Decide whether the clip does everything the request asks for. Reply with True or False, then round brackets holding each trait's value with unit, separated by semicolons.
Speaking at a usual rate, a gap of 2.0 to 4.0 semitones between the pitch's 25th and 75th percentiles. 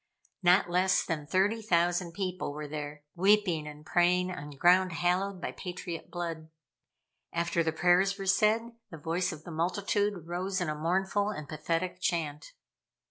True (155 wpm; 2.8 semitones)